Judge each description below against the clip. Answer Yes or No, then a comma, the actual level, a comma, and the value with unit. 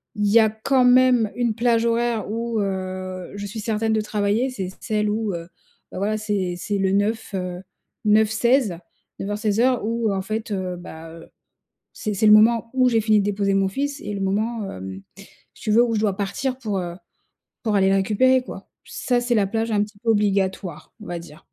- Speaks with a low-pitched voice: No, high, 210 Hz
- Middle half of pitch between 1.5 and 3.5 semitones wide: Yes, average, 2.9 semitones